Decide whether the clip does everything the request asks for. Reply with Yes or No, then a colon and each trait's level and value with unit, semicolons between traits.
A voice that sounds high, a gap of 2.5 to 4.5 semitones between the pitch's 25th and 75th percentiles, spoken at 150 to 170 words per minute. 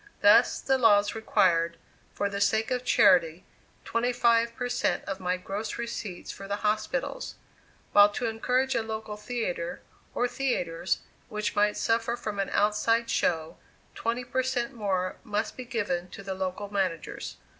Yes: high, 210 Hz; average, 3.5 semitones; average, 155 wpm